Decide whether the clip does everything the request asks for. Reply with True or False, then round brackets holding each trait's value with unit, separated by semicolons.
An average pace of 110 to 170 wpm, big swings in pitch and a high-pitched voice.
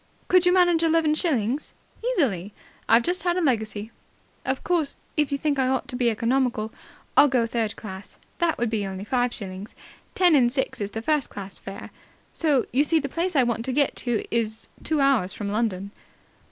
False (195 wpm; 5.8 semitones; 250 Hz)